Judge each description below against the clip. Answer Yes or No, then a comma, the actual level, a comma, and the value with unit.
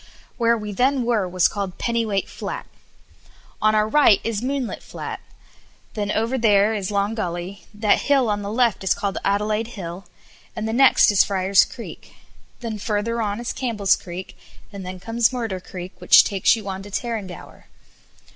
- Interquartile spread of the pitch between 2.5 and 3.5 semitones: Yes, average, 2.9 semitones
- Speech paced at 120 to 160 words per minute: No, average, 170 wpm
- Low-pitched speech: No, high, 210 Hz